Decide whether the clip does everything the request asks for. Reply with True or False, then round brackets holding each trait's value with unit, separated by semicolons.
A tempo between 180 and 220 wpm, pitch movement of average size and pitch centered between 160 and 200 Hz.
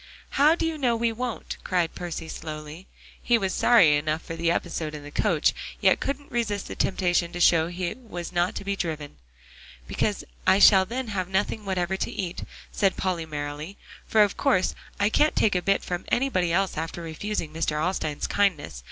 True (190 wpm; 4.3 semitones; 185 Hz)